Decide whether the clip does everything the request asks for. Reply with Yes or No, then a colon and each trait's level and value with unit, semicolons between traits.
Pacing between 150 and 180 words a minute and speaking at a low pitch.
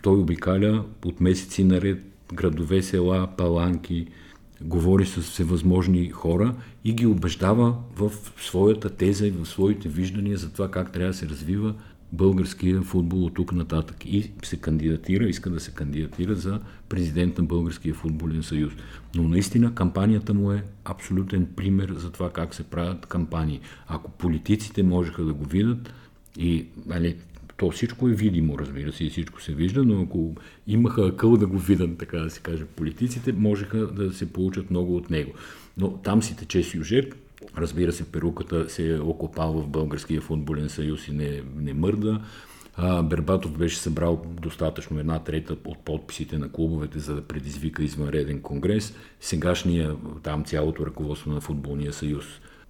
Yes: average, 155 wpm; very low, 85 Hz